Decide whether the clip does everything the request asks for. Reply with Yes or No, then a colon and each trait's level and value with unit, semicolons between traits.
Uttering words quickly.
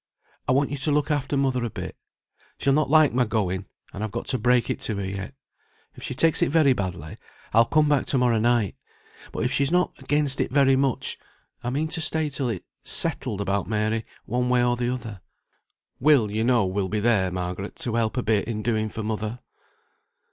Yes: fast, 215 wpm